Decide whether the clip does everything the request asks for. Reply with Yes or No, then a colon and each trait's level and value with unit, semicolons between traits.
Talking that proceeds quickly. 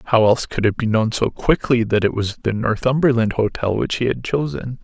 Yes: fast, 225 wpm